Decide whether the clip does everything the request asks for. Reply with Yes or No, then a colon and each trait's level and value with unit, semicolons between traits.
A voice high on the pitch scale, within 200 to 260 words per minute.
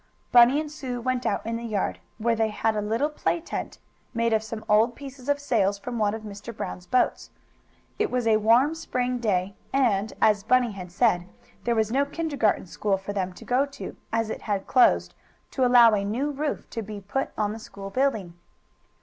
Yes: high, 225 Hz; fast, 205 wpm